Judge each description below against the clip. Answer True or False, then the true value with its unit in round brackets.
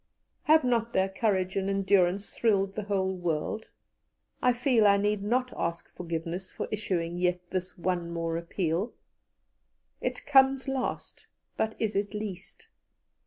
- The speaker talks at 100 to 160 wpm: True (140 wpm)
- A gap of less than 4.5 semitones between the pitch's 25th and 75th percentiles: True (3.6 semitones)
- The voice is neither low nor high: False (195 Hz)